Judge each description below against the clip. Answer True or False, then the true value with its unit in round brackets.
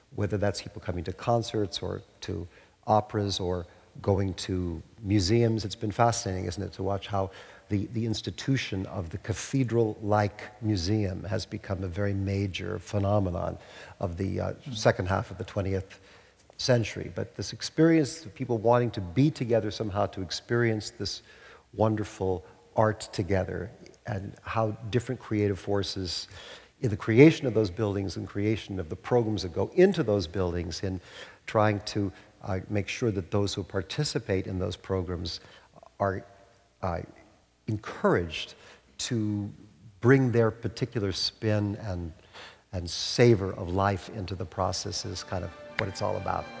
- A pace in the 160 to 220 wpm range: False (150 wpm)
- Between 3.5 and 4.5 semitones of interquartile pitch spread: False (2.6 semitones)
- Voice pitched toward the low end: True (100 Hz)